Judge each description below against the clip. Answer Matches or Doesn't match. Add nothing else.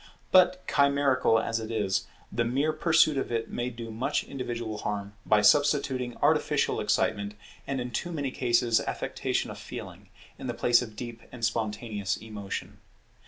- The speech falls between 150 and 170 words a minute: Matches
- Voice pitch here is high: Doesn't match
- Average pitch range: Matches